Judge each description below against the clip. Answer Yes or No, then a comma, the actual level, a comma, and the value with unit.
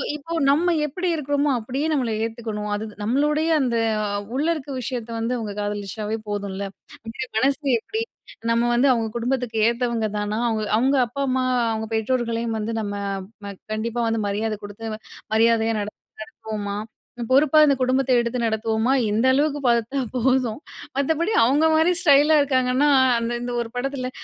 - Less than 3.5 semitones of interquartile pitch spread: No, average, 3.8 semitones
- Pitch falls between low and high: No, high, 235 Hz